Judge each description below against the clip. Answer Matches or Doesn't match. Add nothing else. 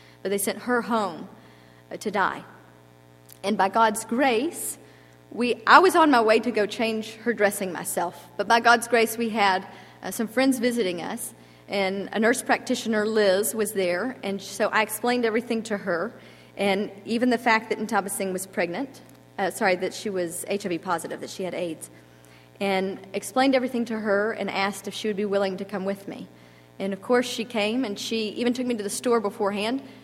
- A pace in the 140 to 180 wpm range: Doesn't match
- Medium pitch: Doesn't match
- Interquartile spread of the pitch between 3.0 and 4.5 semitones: Matches